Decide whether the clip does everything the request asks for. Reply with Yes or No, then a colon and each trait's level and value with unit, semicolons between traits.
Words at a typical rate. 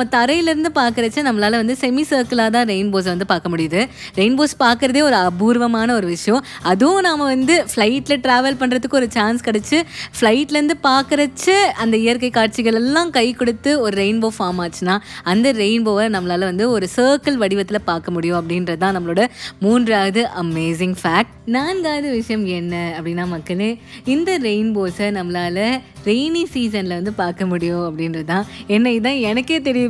No: fast, 145 wpm